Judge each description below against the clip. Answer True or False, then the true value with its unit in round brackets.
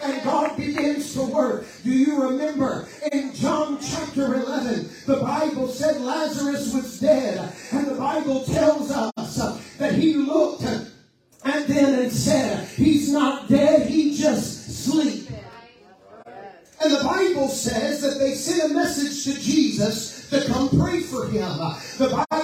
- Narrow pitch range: True (2.2 semitones)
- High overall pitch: True (280 Hz)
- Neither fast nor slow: True (145 wpm)